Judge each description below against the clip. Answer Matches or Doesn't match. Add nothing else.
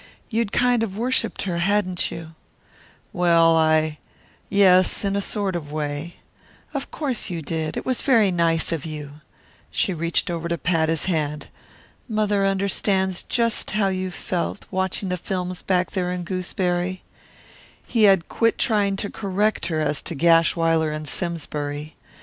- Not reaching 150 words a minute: Doesn't match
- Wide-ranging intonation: Doesn't match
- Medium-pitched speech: Matches